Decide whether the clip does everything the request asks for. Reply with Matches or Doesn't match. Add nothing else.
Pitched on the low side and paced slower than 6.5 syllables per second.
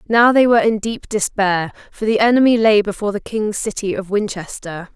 Doesn't match